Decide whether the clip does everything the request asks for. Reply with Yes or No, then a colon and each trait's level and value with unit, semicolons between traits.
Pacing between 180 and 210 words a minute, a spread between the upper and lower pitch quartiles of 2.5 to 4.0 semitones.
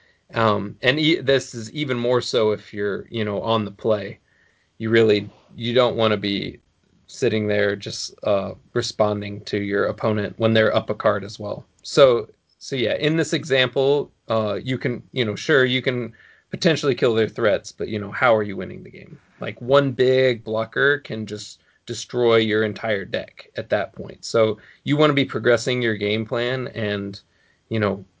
Yes: average, 190 wpm; average, 3.4 semitones